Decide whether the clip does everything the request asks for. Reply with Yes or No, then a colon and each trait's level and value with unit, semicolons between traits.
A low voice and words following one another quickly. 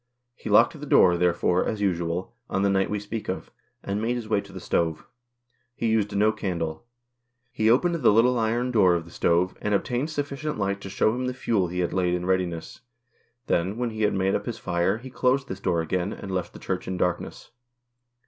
Yes: low, 100 Hz; fast, 215 wpm